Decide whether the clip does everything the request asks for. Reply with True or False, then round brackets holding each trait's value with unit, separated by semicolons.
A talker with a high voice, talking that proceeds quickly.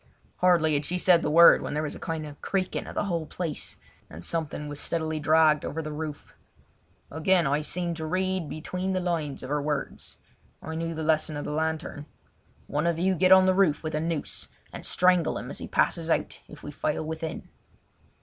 False (160 Hz; 210 wpm)